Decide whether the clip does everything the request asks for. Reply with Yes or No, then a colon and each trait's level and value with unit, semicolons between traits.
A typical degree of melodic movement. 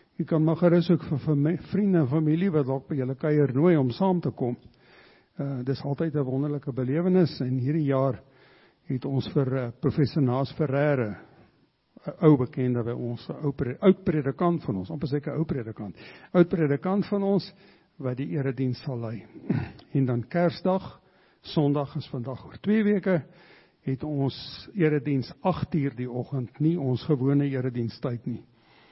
Yes: average, 4.1 semitones